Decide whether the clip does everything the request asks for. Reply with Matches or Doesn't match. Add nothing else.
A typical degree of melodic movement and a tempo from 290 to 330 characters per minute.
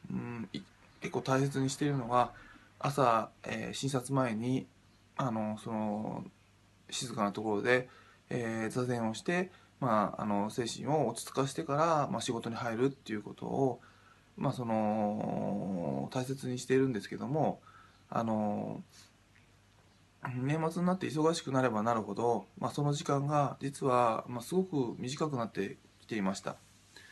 Doesn't match